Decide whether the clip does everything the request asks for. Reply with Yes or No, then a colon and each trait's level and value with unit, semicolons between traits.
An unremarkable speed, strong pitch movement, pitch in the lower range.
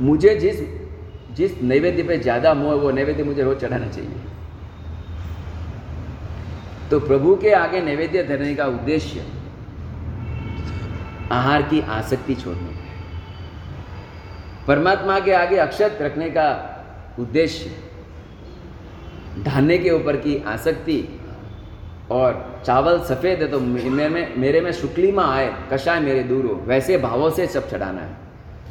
Yes: average, 120 wpm; wide, 8.2 semitones; low, 125 Hz